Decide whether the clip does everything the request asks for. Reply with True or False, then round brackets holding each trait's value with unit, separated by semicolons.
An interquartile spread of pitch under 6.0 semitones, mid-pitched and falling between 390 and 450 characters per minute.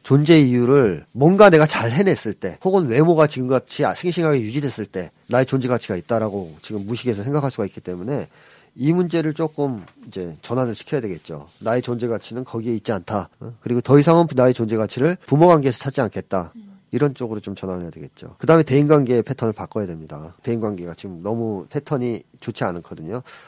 False (5.5 semitones; 125 Hz; 420 characters per minute)